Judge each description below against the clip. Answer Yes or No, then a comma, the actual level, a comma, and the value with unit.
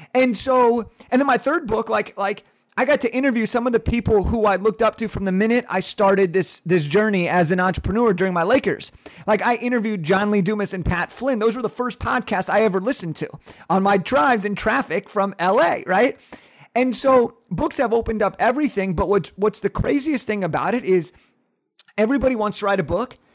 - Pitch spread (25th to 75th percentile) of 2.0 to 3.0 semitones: No, average, 4.1 semitones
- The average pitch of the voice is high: Yes, high, 215 Hz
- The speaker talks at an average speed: No, fast, 215 wpm